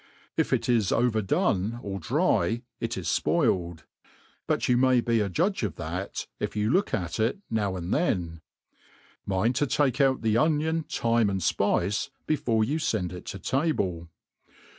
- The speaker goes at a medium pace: Yes, average, 160 wpm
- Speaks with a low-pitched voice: Yes, low, 110 Hz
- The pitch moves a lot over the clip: Yes, wide, 5.7 semitones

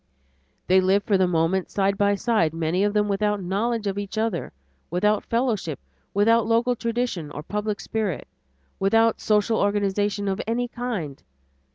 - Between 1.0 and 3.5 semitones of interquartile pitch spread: Yes, average, 2.9 semitones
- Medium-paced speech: Yes, average, 155 wpm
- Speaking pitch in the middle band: No, high, 205 Hz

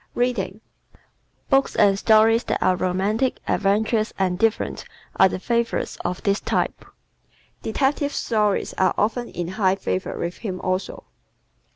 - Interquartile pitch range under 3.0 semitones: No, average, 3.4 semitones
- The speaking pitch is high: Yes, high, 210 Hz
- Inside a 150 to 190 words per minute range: No, average, 140 wpm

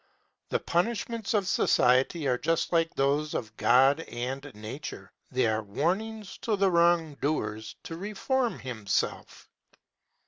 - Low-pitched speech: No, medium, 155 Hz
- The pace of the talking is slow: Yes, slow, 130 wpm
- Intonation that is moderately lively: No, wide, 7.1 semitones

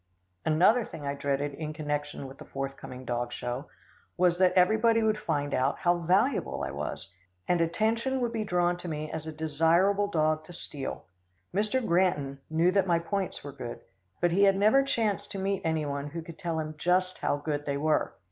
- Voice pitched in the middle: Yes, medium, 165 Hz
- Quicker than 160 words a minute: Yes, average, 195 wpm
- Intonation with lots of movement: No, average, 5.0 semitones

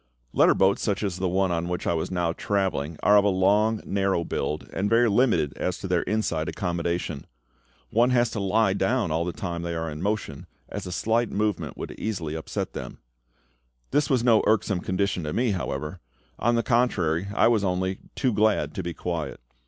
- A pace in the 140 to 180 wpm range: No, average, 200 wpm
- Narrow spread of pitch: No, average, 4.1 semitones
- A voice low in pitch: Yes, very low, 95 Hz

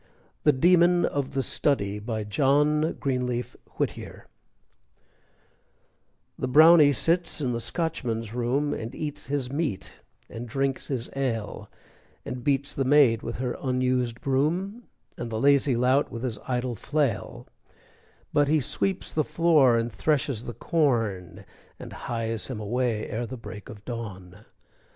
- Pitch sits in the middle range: No, low, 130 Hz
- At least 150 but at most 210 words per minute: No, average, 140 wpm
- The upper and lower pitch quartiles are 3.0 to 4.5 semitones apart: Yes, average, 4.1 semitones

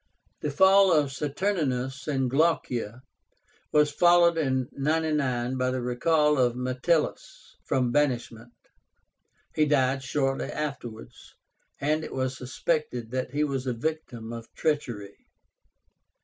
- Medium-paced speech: No, slow, 120 wpm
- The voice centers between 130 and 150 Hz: Yes, low, 135 Hz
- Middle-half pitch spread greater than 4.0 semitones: No, average, 3.3 semitones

